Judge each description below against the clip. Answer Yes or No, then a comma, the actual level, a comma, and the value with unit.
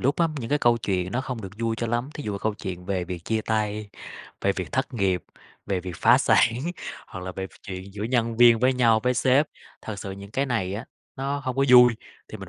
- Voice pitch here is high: No, low, 110 Hz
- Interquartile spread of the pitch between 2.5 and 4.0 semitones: No, average, 4.5 semitones